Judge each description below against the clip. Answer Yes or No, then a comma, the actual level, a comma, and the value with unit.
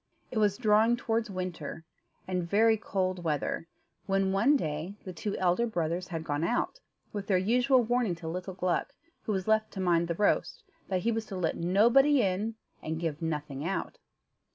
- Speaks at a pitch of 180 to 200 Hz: Yes, high, 190 Hz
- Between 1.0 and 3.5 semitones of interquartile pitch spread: No, average, 4.4 semitones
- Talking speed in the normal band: Yes, average, 180 wpm